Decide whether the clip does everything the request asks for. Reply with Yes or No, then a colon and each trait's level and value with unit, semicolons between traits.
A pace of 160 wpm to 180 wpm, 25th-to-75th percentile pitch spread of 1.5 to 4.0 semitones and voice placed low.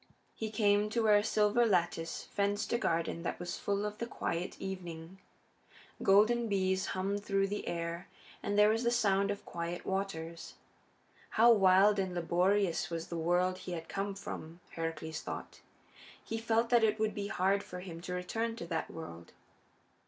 No: average, 175 wpm; average, 3.4 semitones; high, 195 Hz